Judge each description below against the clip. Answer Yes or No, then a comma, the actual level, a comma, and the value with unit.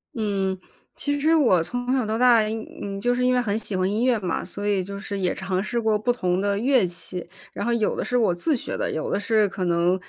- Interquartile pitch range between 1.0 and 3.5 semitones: No, average, 4.3 semitones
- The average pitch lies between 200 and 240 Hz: Yes, high, 210 Hz